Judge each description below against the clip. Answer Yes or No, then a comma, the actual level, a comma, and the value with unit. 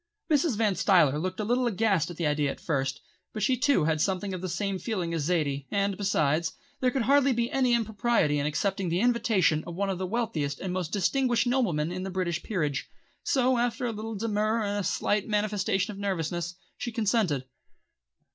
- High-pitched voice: Yes, high, 195 Hz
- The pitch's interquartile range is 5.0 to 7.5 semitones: Yes, average, 5.3 semitones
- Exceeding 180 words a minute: Yes, average, 200 wpm